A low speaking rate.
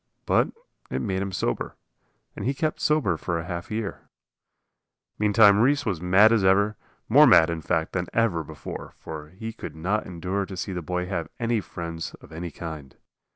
No: average, 185 wpm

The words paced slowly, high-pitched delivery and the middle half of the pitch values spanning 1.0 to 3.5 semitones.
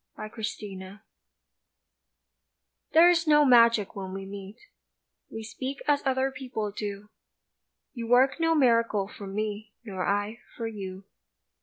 No: slow, 130 wpm; high, 220 Hz; average, 4.4 semitones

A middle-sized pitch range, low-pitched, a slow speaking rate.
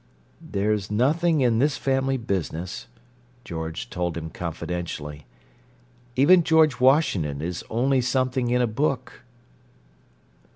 No: wide, 7.3 semitones; low, 120 Hz; slow, 110 wpm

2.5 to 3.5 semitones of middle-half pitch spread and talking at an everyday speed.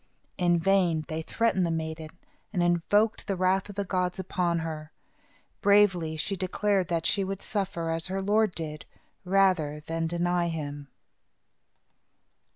Yes: average, 3.0 semitones; average, 145 wpm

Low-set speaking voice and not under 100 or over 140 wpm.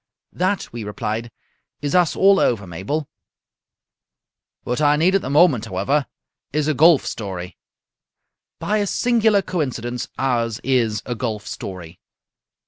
Yes: low, 130 Hz; slow, 135 wpm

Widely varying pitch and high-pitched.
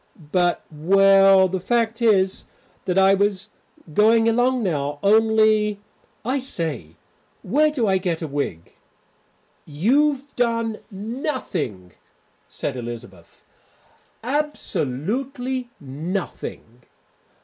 Yes: wide, 6.7 semitones; high, 195 Hz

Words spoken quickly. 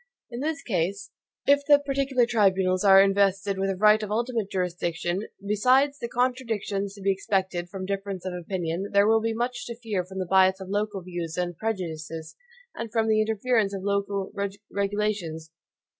No: average, 175 wpm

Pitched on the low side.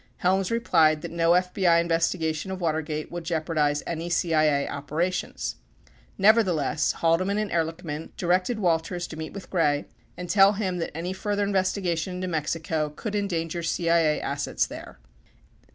No: medium, 170 Hz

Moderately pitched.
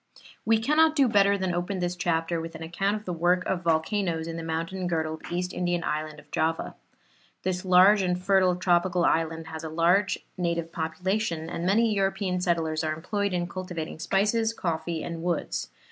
Yes: medium, 175 Hz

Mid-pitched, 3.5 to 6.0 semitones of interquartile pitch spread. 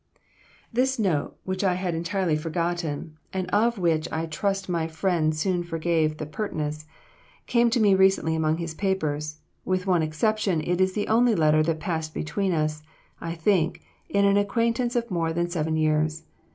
Yes: medium, 170 Hz; average, 3.8 semitones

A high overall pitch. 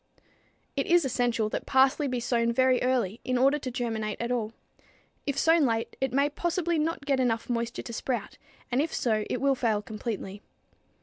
Yes: very high, 250 Hz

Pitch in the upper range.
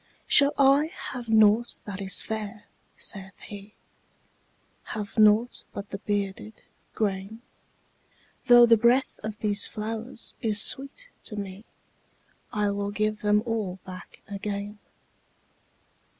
Yes: high, 210 Hz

